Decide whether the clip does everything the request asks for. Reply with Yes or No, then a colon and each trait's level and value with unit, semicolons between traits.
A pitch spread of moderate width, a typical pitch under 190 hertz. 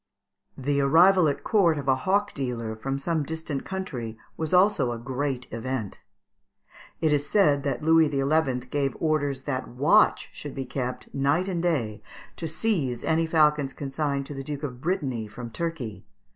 Yes: average, 3.9 semitones; medium, 140 Hz